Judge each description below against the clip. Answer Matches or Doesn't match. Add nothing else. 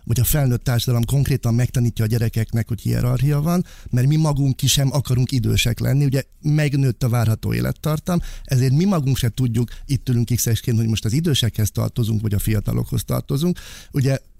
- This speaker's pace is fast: Matches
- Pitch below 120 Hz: Doesn't match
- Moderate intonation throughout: Matches